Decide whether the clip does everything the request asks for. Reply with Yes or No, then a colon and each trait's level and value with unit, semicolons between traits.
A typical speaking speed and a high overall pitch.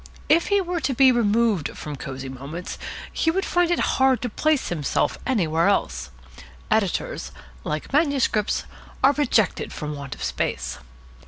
Yes: average, 150 wpm; high, 230 Hz